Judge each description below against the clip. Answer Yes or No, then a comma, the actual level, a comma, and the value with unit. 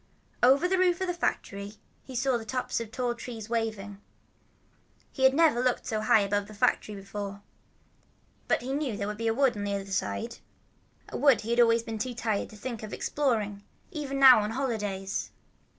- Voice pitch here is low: No, high, 230 Hz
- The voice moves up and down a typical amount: Yes, average, 4.1 semitones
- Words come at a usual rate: Yes, average, 190 wpm